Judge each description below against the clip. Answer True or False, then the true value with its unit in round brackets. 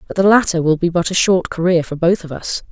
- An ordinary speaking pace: False (290 wpm)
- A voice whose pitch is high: False (175 Hz)